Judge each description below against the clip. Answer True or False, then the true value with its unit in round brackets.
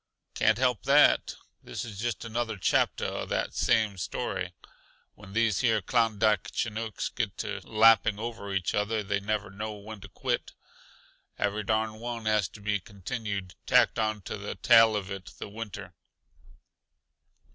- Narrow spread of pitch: True (2.0 semitones)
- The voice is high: False (110 Hz)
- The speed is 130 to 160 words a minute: True (155 wpm)